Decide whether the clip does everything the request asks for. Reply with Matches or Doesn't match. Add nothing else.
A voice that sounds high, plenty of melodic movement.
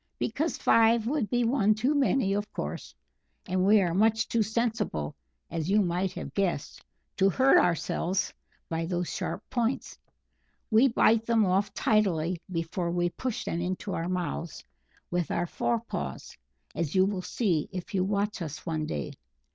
Doesn't match